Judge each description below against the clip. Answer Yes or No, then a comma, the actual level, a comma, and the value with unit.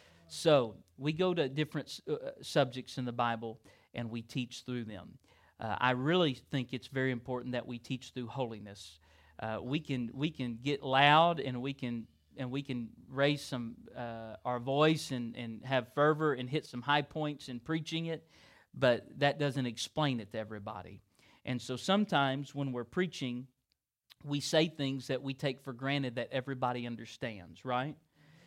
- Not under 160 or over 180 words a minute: Yes, average, 175 wpm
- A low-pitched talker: Yes, low, 130 Hz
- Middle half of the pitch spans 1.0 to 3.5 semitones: Yes, average, 3.2 semitones